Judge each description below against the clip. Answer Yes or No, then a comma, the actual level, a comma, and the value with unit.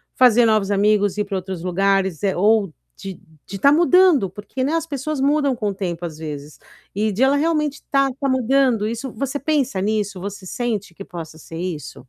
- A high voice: Yes, high, 215 Hz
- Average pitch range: No, wide, 6.0 semitones